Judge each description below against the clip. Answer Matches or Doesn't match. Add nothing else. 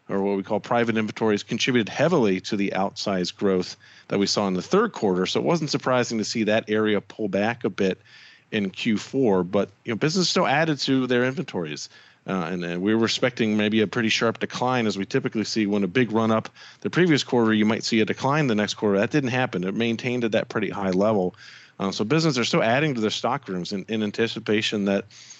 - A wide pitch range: Doesn't match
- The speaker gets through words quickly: Matches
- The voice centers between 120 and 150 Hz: Doesn't match